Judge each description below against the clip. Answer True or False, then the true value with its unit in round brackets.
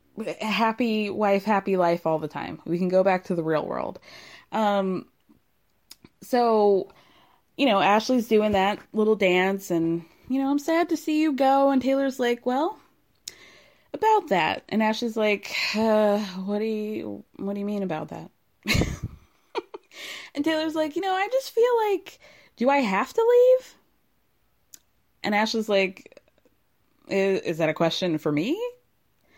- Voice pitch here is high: True (215 Hz)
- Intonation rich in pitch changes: True (6.7 semitones)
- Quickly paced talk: False (155 wpm)